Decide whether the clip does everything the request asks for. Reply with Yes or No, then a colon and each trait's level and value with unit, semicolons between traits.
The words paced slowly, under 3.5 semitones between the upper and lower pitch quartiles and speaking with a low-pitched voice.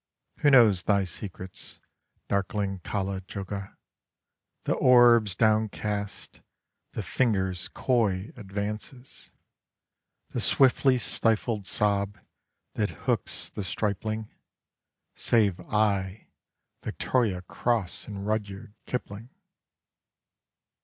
Yes: slow, 85 wpm; narrow, 2.5 semitones; low, 105 Hz